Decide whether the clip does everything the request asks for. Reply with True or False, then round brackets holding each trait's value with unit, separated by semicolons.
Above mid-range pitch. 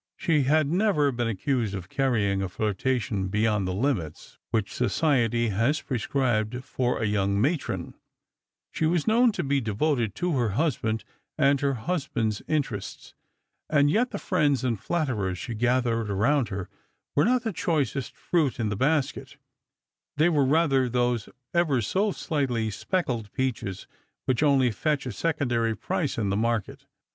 False (130 Hz)